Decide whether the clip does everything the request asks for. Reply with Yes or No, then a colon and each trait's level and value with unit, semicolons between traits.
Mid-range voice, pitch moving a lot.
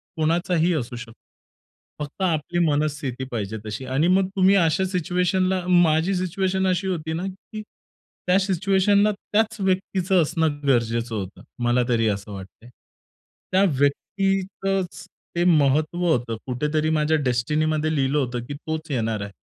Yes: medium, 160 Hz; wide, 6.2 semitones